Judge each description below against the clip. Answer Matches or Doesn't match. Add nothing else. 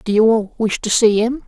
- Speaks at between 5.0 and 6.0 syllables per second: Doesn't match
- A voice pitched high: Matches